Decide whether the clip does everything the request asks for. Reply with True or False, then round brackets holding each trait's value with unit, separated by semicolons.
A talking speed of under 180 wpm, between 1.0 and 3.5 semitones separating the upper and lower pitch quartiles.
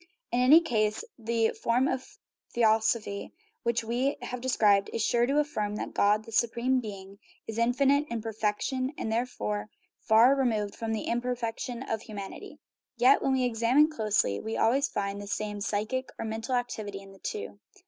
True (170 wpm; 3.1 semitones)